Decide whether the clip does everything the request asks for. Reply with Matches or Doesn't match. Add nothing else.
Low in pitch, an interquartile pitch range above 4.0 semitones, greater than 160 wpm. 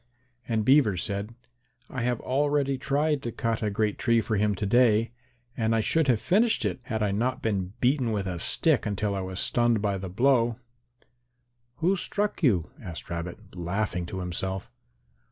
Matches